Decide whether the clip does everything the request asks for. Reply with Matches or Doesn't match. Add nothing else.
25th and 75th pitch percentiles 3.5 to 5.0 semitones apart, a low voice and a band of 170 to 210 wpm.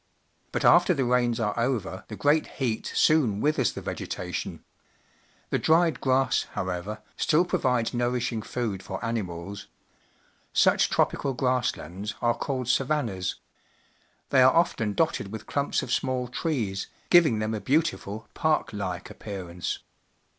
Doesn't match